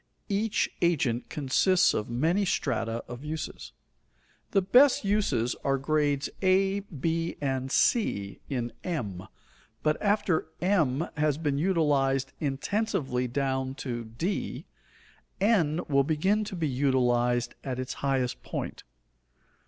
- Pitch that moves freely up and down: Yes, wide, 6.2 semitones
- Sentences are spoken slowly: Yes, slow, 120 wpm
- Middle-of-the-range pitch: Yes, medium, 145 Hz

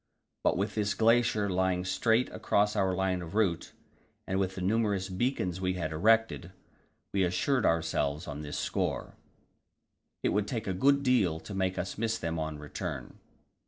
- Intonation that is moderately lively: Yes, average, 3.7 semitones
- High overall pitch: No, very low, 95 Hz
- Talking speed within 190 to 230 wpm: No, average, 170 wpm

